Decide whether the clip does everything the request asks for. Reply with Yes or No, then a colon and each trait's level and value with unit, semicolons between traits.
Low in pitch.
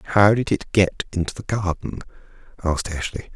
Yes: very low, 95 Hz